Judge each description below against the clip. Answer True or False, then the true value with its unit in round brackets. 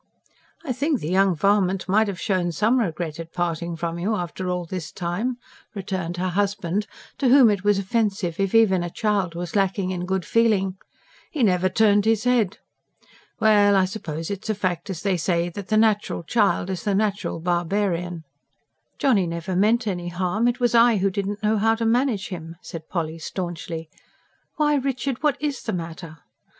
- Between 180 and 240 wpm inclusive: True (185 wpm)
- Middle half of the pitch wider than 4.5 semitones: False (3.8 semitones)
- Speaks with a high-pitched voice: True (195 Hz)